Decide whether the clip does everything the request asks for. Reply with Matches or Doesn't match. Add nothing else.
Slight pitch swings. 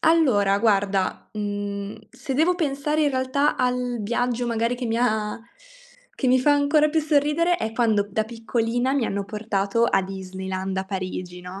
Doesn't match